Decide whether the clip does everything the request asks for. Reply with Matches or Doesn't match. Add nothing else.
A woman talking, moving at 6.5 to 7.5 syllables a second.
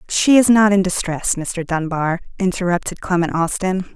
Doesn't match